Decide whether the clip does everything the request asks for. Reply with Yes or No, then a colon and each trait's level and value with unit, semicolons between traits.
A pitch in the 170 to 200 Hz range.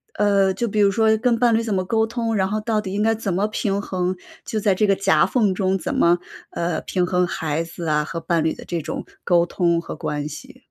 Yes: high, 195 Hz